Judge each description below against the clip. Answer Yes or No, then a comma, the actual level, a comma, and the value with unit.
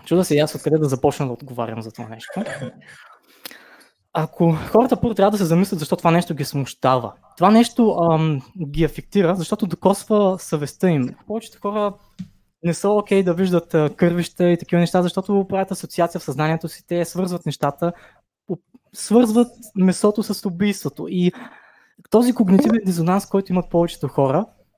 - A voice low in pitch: No, medium, 180 Hz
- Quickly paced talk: No, average, 155 wpm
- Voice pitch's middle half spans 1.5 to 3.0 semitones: No, average, 4.2 semitones